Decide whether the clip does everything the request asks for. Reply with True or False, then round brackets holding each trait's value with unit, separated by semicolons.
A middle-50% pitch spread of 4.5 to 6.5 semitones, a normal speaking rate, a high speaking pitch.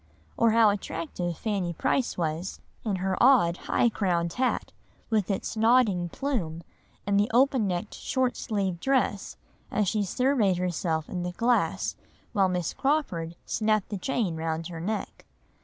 True (4.9 semitones; 150 wpm; 200 Hz)